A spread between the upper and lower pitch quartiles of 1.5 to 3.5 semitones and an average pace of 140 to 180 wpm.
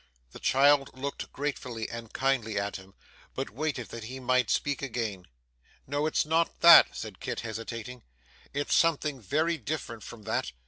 No: average, 4.3 semitones; average, 155 wpm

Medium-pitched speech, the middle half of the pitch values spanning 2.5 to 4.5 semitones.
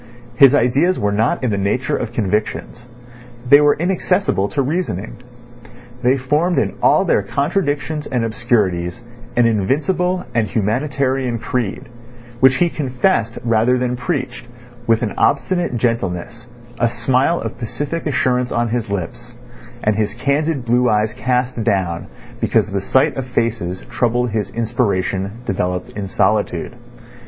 No: low, 120 Hz; average, 3.8 semitones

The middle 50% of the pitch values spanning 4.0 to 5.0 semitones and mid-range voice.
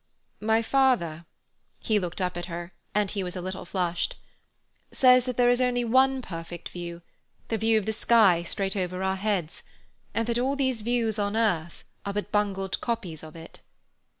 No: average, 4.7 semitones; high, 205 Hz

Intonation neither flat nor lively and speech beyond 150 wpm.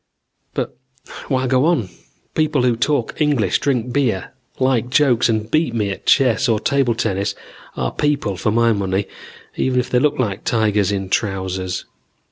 Yes: average, 4.5 semitones; average, 160 wpm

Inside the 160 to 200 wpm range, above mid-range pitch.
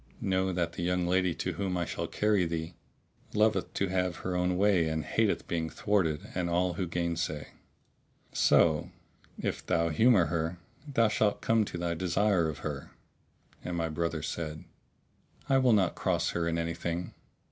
No: average, 170 wpm; very low, 85 Hz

